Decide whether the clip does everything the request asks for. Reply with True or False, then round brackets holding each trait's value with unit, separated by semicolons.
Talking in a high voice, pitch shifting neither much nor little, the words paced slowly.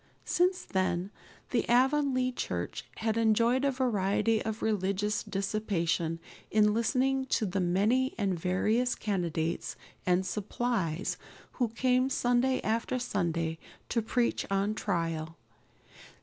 True (215 Hz; 4.9 semitones; 115 wpm)